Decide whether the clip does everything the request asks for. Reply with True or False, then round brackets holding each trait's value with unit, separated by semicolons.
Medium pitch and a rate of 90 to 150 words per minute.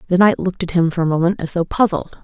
False (175 Hz; 295 wpm)